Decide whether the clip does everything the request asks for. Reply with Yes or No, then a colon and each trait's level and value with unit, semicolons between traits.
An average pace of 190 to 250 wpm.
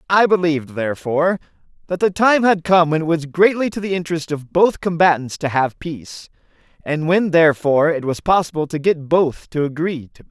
Yes: average, 200 wpm